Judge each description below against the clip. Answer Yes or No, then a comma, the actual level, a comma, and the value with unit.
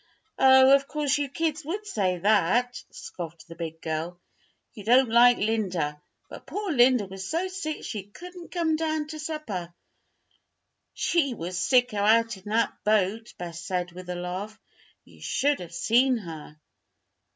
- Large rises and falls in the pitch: Yes, wide, 7.7 semitones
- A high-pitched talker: Yes, high, 225 Hz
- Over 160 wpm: No, average, 155 wpm